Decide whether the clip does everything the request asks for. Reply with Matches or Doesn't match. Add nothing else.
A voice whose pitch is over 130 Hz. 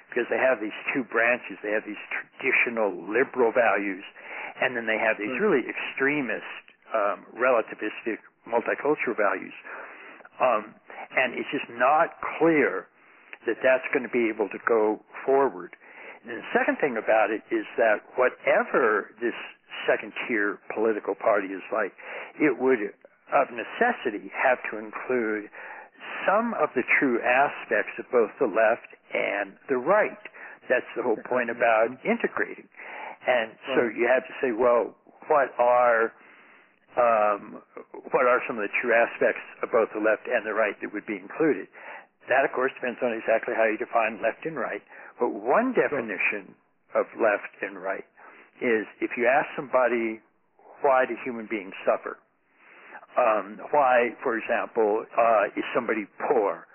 Doesn't match